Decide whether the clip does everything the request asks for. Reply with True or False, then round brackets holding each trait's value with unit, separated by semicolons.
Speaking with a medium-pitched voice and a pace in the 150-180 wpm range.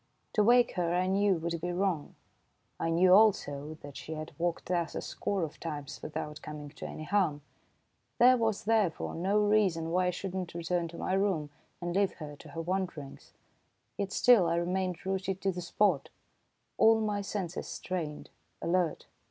True (180 Hz; 175 wpm)